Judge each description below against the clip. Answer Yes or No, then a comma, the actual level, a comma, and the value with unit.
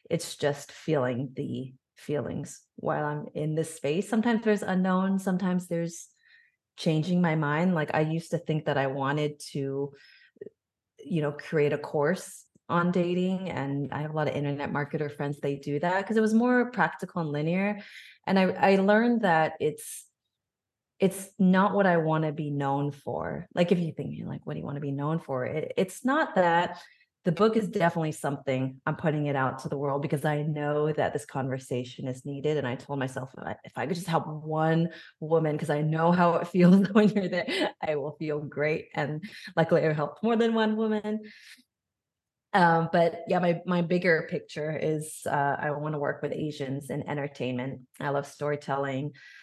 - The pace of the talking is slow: No, average, 190 wpm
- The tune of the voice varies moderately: Yes, average, 4.3 semitones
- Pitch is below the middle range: No, medium, 160 Hz